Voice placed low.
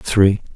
Yes: low, 100 Hz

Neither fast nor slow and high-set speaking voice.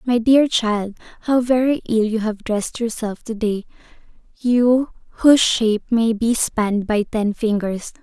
Yes: average, 150 wpm; high, 225 Hz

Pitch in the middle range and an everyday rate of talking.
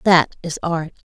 Yes: medium, 165 Hz; average, 160 wpm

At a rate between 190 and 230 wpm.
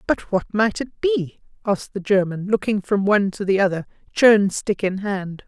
Yes: average, 195 wpm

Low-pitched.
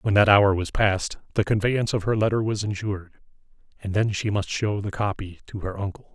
Yes: low, 100 Hz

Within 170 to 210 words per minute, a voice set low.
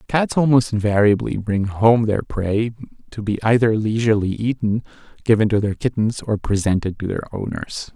No: average, 160 wpm; low, 110 Hz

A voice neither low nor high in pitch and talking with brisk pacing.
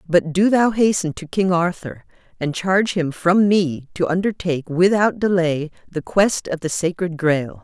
No: medium, 175 Hz; average, 175 wpm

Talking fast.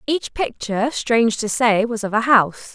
No: average, 195 wpm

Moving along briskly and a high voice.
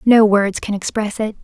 Yes: fast, 210 wpm; high, 210 Hz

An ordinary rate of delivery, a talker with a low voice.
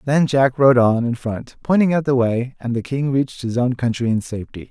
No: fast, 240 wpm; low, 125 Hz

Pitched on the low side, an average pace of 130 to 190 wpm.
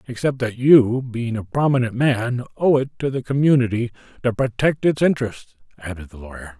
Yes: low, 120 Hz; average, 175 wpm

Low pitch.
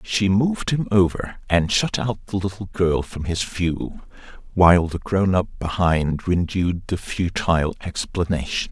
Yes: very low, 90 Hz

